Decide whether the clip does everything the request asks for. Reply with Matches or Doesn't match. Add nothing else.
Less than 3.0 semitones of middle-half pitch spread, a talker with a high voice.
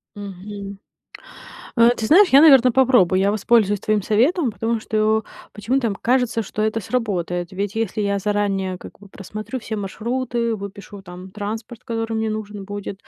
Matches